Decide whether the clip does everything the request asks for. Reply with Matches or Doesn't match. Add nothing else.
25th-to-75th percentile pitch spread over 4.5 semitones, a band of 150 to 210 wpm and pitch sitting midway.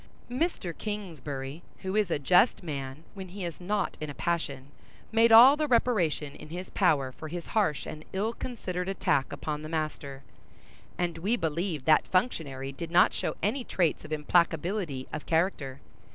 Matches